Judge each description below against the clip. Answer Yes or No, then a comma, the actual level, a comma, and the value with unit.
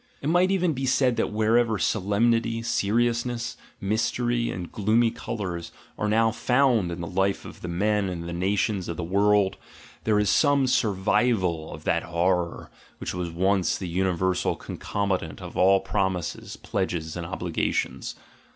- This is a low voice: Yes, low, 100 Hz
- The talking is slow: No, average, 150 wpm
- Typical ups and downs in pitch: Yes, average, 4.4 semitones